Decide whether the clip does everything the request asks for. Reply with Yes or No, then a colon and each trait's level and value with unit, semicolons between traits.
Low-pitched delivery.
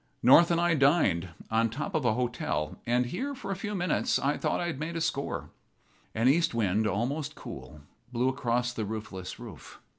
Yes: low, 130 Hz